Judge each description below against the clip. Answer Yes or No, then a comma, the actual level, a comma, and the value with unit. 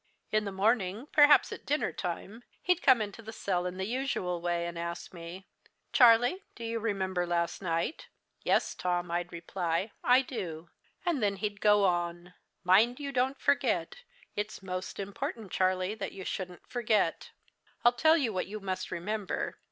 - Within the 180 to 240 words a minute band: No, average, 165 wpm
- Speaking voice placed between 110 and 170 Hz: No, high, 195 Hz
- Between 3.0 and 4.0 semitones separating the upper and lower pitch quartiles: No, average, 4.5 semitones